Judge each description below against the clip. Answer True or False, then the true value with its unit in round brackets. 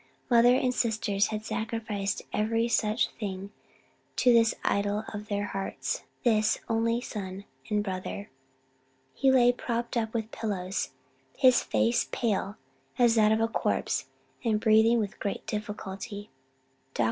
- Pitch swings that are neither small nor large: False (2.2 semitones)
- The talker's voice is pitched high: True (220 Hz)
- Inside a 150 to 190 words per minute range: False (135 wpm)